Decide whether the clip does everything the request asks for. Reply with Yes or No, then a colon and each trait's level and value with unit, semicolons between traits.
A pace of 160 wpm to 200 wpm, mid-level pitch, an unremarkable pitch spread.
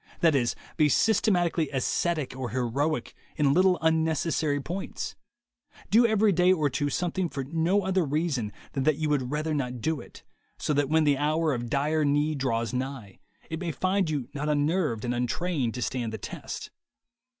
Yes: average, 175 wpm; medium, 150 Hz; average, 3.9 semitones